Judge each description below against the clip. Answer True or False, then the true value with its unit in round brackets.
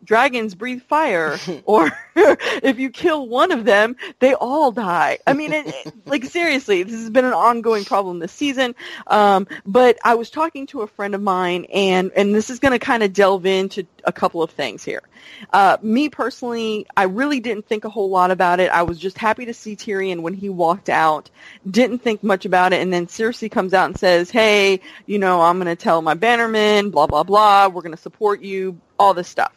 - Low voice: False (210 Hz)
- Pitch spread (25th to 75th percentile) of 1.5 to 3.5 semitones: False (4.6 semitones)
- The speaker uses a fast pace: True (215 wpm)